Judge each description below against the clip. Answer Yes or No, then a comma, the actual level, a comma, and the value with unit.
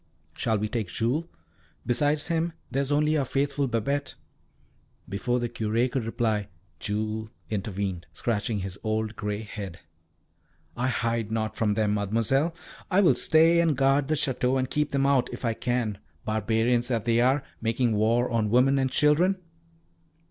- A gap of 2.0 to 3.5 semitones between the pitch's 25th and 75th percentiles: No, average, 4.2 semitones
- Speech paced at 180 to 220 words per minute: No, average, 160 wpm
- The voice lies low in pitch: Yes, low, 120 Hz